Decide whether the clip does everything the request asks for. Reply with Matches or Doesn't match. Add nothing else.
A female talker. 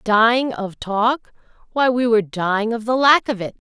Matches